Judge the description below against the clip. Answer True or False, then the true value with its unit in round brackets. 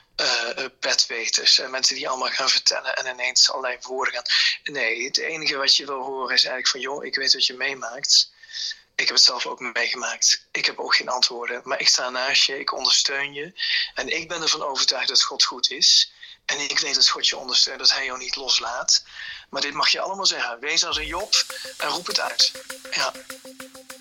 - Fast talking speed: True (205 wpm)